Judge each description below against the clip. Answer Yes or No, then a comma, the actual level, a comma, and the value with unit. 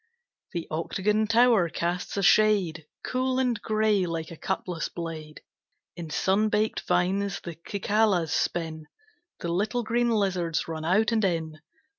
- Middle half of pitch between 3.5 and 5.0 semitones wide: Yes, average, 4.5 semitones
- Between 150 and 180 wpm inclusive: No, average, 140 wpm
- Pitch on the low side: No, high, 190 Hz